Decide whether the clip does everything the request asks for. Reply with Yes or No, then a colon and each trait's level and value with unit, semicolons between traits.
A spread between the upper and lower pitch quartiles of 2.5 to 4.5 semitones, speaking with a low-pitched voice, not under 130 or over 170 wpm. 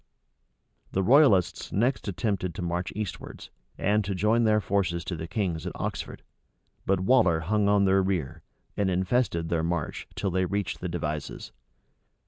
Yes: average, 3.2 semitones; very low, 95 Hz; average, 155 wpm